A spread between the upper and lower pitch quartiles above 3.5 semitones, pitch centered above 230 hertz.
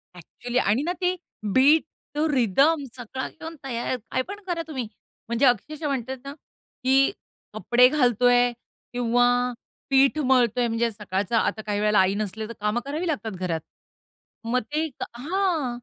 Yes: average, 3.9 semitones; very high, 250 Hz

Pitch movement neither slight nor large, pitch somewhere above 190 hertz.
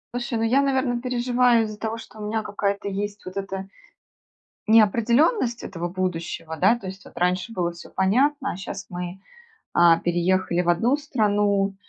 Yes: average, 4.3 semitones; high, 205 Hz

